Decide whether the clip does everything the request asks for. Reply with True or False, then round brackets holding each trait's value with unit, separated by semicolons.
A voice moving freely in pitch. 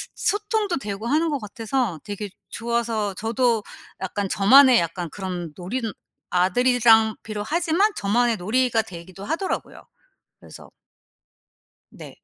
False (4.6 semitones)